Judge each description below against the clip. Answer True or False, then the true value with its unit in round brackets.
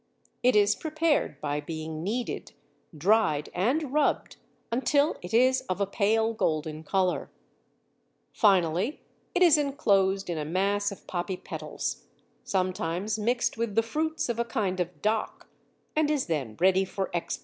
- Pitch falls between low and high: False (200 Hz)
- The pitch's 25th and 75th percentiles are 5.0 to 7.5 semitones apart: True (5.3 semitones)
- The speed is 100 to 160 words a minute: True (150 wpm)